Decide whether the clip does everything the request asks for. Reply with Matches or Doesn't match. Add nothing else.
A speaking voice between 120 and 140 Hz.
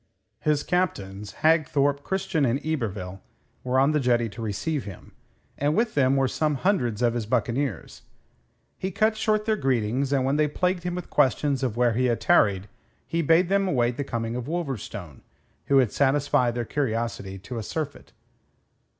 Matches